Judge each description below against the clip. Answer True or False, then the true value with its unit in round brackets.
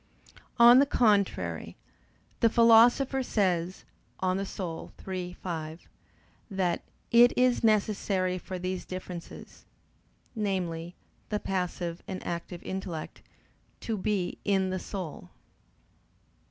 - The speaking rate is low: True (100 wpm)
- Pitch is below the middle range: False (190 Hz)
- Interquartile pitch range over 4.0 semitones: False (3.3 semitones)